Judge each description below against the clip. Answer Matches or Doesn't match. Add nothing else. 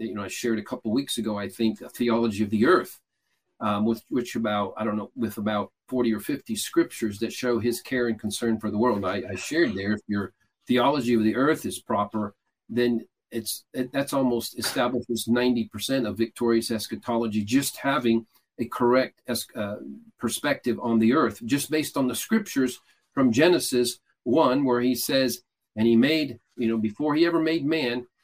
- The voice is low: Matches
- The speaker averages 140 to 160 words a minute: Doesn't match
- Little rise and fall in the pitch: Matches